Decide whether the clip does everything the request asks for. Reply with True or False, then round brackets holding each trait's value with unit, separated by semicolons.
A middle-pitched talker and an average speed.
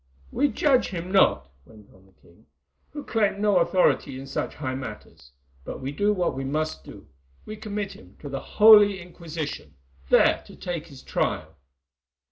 True (165 Hz; 165 wpm)